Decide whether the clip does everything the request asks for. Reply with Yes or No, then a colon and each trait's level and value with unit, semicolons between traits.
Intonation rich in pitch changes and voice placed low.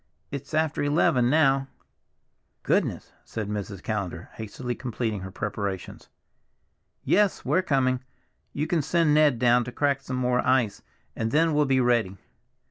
No: average, 4.8 semitones; low, 130 Hz